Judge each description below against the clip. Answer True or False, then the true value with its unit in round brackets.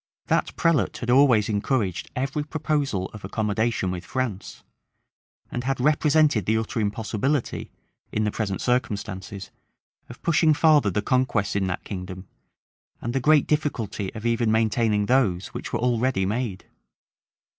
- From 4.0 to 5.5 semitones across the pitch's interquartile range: True (4.8 semitones)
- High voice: False (115 Hz)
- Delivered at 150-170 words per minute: False (140 wpm)